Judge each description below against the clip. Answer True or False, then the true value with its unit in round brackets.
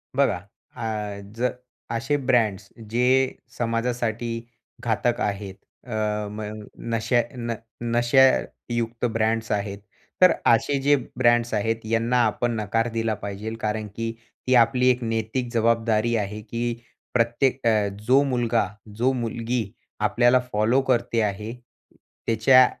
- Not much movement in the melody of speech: True (2.0 semitones)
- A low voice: True (115 Hz)